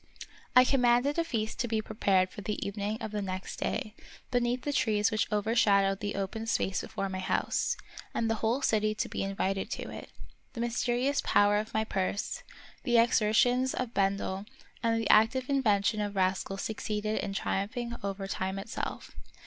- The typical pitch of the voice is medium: No, high, 215 Hz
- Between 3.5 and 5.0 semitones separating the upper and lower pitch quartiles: No, average, 3.1 semitones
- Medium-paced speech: Yes, average, 180 wpm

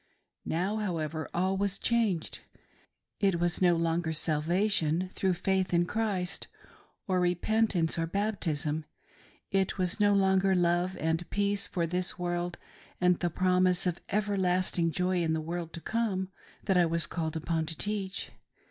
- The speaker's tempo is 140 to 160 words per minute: Yes, average, 155 wpm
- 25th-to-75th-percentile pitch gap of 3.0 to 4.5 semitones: No, narrow, 2.5 semitones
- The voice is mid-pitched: Yes, medium, 180 Hz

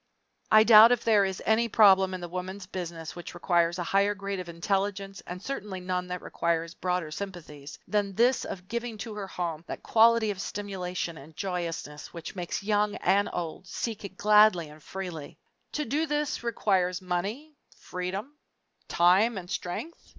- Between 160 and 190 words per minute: Yes, average, 170 wpm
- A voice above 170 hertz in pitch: Yes, high, 190 Hz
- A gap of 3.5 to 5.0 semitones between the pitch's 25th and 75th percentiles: No, average, 3.1 semitones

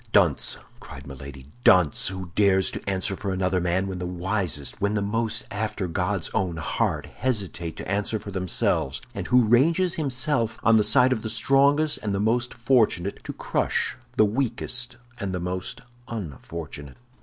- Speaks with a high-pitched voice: No, low, 100 Hz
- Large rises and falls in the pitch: No, average, 4.5 semitones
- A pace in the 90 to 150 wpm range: No, average, 165 wpm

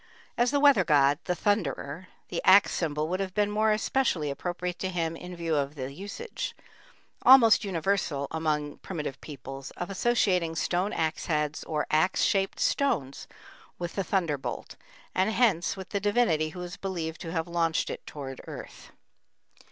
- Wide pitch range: No, average, 4.3 semitones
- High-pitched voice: No, medium, 175 Hz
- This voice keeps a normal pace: Yes, average, 165 wpm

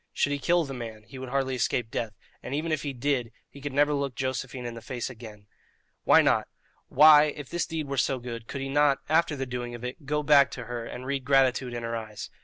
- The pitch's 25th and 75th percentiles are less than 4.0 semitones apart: Yes, average, 3.1 semitones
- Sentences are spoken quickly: Yes, fast, 245 wpm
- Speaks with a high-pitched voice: No, low, 130 Hz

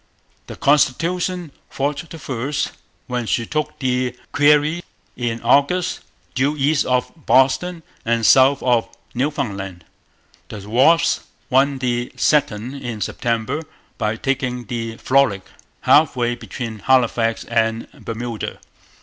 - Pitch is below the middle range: Yes, low, 130 Hz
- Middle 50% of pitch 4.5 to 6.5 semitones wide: No, average, 3.9 semitones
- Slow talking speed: Yes, slow, 115 wpm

